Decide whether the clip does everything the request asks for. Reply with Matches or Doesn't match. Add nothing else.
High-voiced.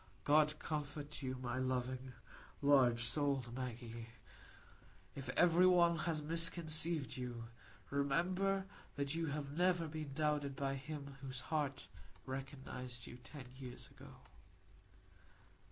Doesn't match